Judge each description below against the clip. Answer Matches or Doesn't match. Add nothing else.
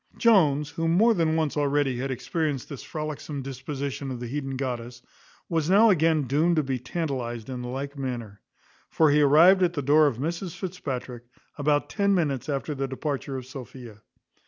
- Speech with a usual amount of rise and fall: Matches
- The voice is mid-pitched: Matches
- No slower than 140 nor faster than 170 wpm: Doesn't match